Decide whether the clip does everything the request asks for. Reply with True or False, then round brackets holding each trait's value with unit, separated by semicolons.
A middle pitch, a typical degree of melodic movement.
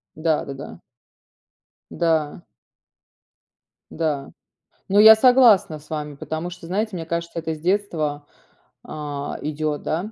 True (160 Hz; 3.4 semitones)